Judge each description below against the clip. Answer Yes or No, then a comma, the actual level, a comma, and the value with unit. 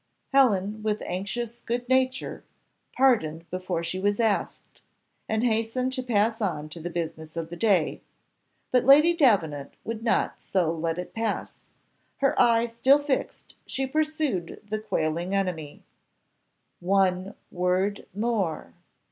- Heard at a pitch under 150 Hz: No, high, 205 Hz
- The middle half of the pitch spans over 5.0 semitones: Yes, wide, 5.4 semitones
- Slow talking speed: Yes, slow, 130 wpm